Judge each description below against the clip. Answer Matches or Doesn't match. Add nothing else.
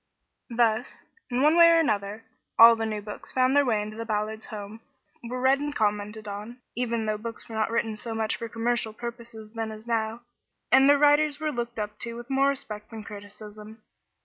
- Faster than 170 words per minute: Matches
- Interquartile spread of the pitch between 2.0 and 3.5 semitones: Matches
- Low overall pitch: Doesn't match